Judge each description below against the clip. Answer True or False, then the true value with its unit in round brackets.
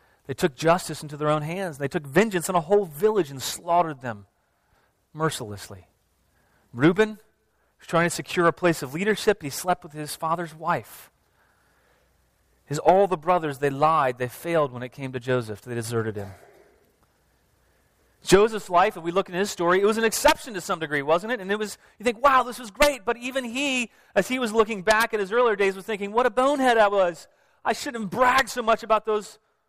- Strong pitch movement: True (7.1 semitones)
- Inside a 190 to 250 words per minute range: True (205 wpm)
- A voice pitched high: False (175 Hz)